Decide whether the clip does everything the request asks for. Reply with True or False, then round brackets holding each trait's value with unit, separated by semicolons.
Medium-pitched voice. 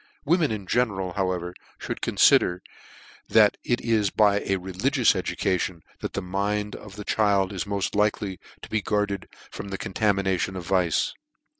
False (100 Hz)